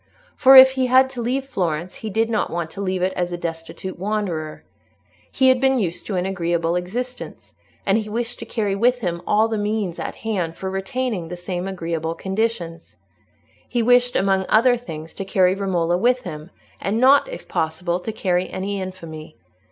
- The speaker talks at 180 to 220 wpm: Yes, average, 190 wpm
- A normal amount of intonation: Yes, average, 4.9 semitones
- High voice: Yes, high, 195 Hz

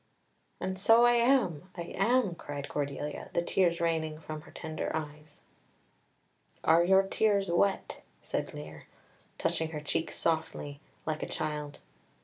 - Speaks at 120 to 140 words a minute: Yes, slow, 135 wpm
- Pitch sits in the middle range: Yes, medium, 165 Hz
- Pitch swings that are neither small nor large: Yes, average, 4.1 semitones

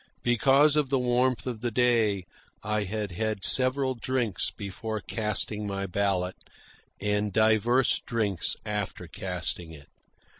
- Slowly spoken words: Yes, slow, 125 wpm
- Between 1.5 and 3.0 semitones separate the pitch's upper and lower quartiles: No, average, 3.4 semitones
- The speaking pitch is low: Yes, low, 110 Hz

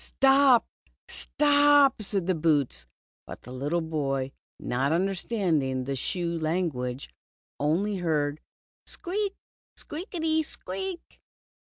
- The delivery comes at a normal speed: No, slow, 110 wpm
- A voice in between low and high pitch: Yes, medium, 170 Hz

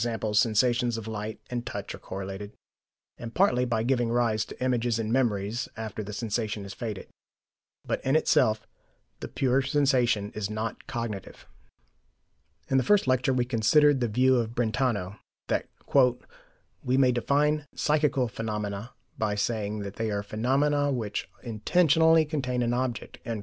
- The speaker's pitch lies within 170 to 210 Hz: No, low, 120 Hz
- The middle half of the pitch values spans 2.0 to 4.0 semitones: Yes, average, 3.3 semitones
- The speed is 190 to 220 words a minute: No, average, 145 wpm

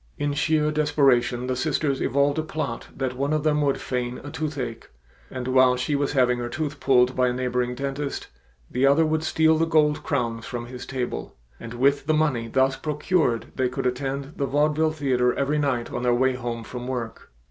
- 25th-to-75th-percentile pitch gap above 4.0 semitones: No, average, 3.1 semitones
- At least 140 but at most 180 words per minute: No, average, 200 wpm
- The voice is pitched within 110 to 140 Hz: Yes, low, 135 Hz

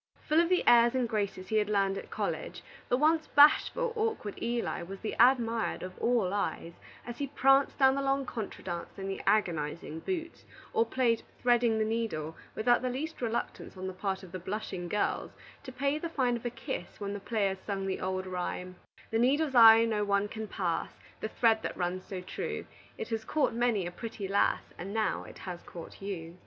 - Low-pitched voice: No, high, 220 Hz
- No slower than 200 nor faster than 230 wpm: Yes, fast, 205 wpm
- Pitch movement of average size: Yes, average, 4.7 semitones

